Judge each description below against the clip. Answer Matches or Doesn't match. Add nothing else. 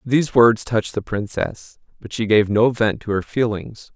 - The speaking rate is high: Doesn't match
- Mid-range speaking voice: Doesn't match